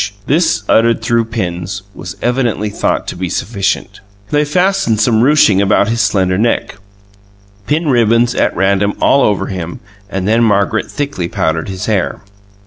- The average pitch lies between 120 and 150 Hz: No, low, 110 Hz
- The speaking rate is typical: Yes, average, 150 wpm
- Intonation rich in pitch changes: No, average, 3.8 semitones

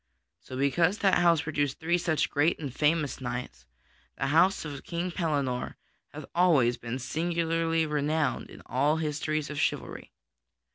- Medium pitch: Yes, medium, 155 Hz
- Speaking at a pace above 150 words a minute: No, average, 145 wpm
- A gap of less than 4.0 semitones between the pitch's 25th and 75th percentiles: Yes, average, 3.2 semitones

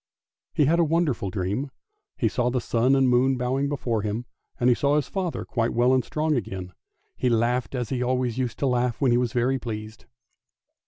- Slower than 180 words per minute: No, fast, 205 wpm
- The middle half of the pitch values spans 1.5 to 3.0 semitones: Yes, narrow, 2.4 semitones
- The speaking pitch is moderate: No, low, 125 Hz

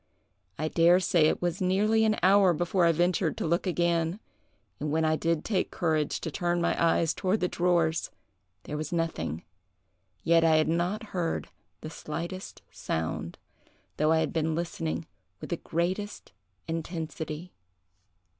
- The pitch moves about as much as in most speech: No, narrow, 2.2 semitones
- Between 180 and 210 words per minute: No, average, 155 wpm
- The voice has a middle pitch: Yes, medium, 170 Hz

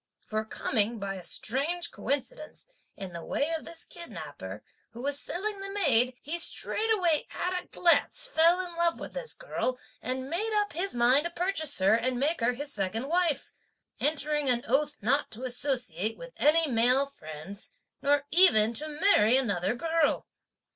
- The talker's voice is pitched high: Yes, very high, 285 Hz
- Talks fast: No, average, 170 wpm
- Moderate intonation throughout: No, wide, 6.2 semitones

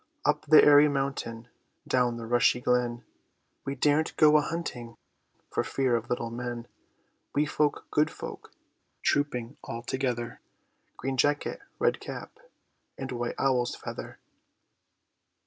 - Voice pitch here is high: No, low, 125 Hz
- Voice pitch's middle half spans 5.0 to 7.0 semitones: No, average, 3.3 semitones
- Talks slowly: Yes, slow, 130 wpm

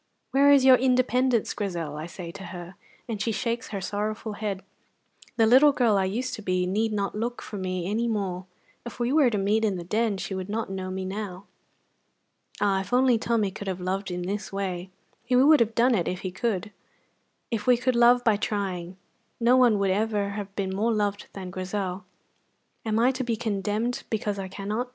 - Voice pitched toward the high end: Yes, high, 210 Hz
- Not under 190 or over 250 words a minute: Yes, fast, 205 wpm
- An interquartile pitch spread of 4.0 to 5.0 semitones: No, average, 3.6 semitones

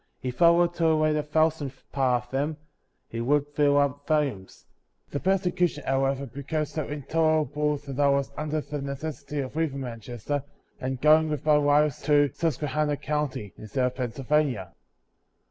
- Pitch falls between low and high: Yes, medium, 145 Hz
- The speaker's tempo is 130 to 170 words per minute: No, average, 180 wpm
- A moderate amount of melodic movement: No, narrow, 2.3 semitones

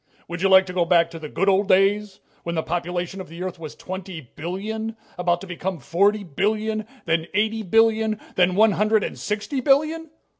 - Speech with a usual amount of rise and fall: Yes, average, 3.6 semitones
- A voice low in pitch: No, high, 190 Hz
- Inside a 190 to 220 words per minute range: Yes, average, 195 wpm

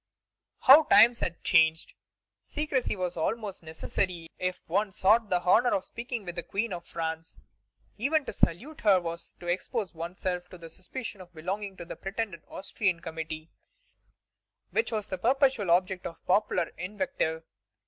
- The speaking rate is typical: Yes, average, 160 wpm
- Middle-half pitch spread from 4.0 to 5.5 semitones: Yes, average, 4.6 semitones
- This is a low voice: No, medium, 185 Hz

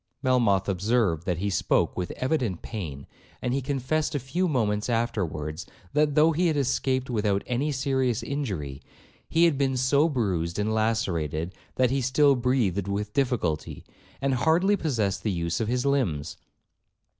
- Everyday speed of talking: Yes, average, 155 wpm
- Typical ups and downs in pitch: No, wide, 6.0 semitones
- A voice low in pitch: Yes, low, 120 Hz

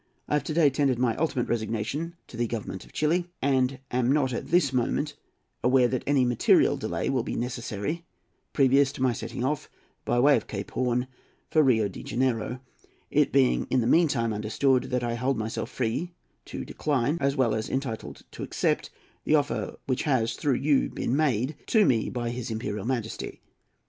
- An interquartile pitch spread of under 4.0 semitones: Yes, average, 3.3 semitones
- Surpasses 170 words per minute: Yes, average, 185 wpm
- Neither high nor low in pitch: No, low, 130 Hz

